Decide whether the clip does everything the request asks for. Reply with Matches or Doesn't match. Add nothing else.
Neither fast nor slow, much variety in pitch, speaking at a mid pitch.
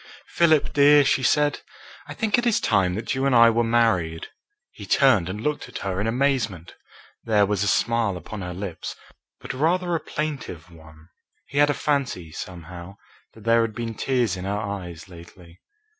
Doesn't match